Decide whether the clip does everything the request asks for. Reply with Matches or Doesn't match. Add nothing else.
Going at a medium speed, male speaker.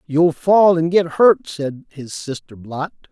Matches